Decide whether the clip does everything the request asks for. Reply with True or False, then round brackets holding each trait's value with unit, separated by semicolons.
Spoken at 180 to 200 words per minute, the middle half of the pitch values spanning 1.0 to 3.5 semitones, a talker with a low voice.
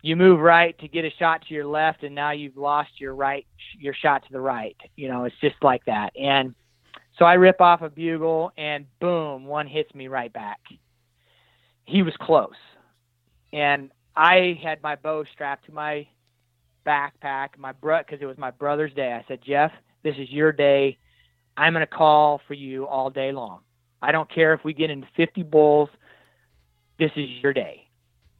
False (190 wpm; 2.8 semitones; 145 Hz)